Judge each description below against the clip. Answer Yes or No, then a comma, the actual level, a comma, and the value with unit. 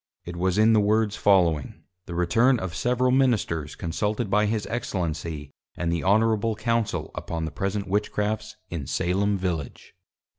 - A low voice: Yes, low, 100 Hz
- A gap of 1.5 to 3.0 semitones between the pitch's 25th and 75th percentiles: No, average, 4.3 semitones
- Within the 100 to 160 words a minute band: Yes, average, 150 wpm